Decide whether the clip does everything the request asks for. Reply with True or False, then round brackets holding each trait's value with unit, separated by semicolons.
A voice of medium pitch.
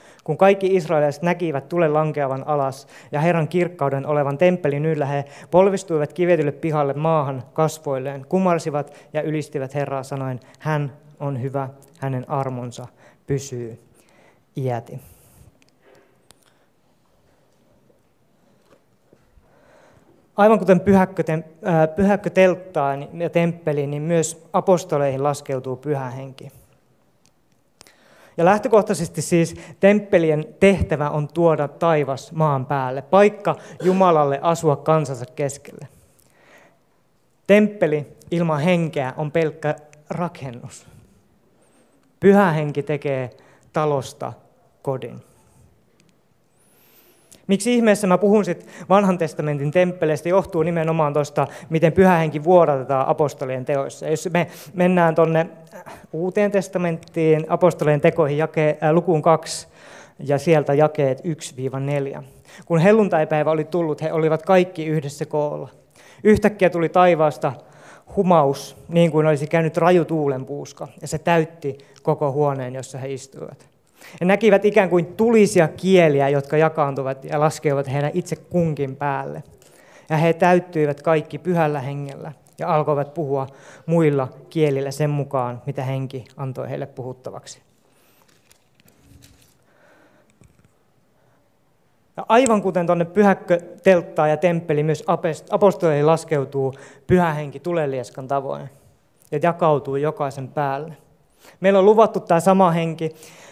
True (155 Hz)